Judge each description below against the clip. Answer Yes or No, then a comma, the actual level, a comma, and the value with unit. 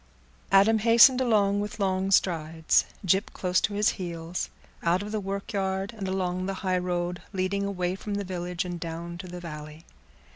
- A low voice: No, medium, 185 Hz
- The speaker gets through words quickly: No, average, 160 wpm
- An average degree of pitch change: No, narrow, 2.2 semitones